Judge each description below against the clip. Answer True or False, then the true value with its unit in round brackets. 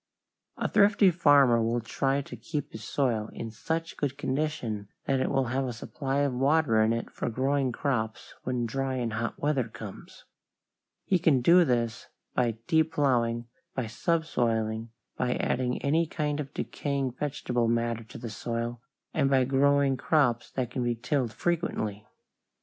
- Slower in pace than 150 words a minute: False (160 wpm)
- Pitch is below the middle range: True (130 Hz)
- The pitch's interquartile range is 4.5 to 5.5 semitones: False (3.5 semitones)